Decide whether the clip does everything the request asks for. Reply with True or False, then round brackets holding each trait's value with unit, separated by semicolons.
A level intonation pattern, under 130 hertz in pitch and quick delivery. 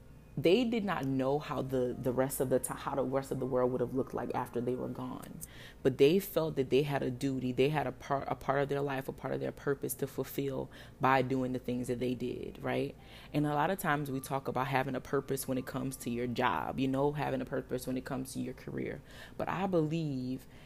False (1.6 semitones; 135 Hz; 255 wpm)